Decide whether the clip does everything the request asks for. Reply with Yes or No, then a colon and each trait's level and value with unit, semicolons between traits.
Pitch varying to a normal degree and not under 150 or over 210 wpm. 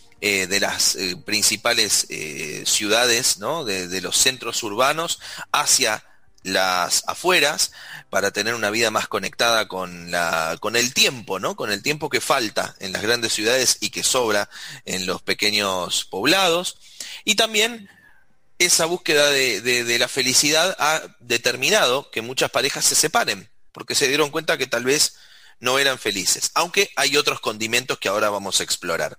No: wide, 6.6 semitones; average, 160 wpm